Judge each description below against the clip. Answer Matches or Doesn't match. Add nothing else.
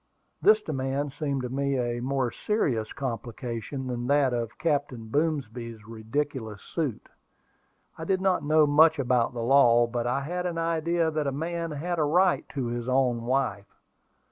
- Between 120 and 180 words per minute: Matches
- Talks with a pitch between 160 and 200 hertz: Doesn't match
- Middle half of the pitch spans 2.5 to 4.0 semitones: Doesn't match